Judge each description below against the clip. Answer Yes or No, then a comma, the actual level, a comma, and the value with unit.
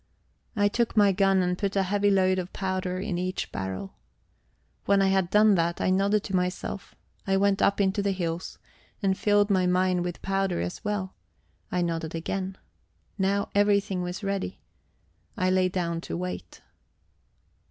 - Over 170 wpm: No, average, 165 wpm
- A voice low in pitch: No, high, 190 Hz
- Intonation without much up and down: Yes, narrow, 1.9 semitones